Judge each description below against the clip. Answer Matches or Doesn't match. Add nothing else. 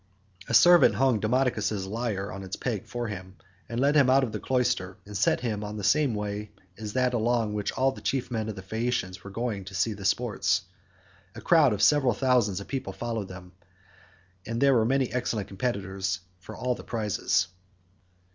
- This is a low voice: Matches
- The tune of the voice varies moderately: Matches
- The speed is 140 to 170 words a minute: Doesn't match